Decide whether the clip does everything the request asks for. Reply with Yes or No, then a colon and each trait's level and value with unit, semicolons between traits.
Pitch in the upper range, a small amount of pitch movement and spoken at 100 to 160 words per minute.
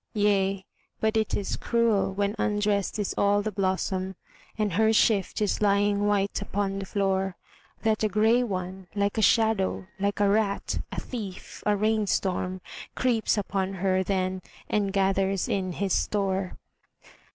Yes: high, 200 Hz; narrow, 1.6 semitones; average, 150 wpm